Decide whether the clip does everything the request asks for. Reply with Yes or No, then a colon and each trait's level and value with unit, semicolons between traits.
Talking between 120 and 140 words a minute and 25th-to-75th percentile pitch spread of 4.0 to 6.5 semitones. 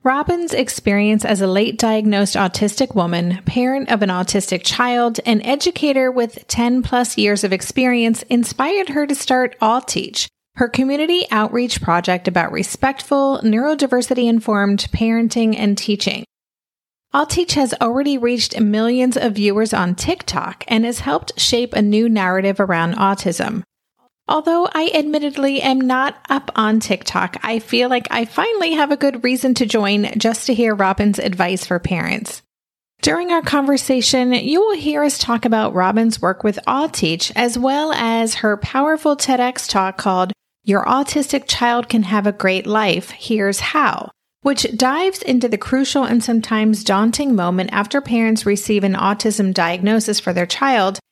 No: average, 155 wpm; average, 4.4 semitones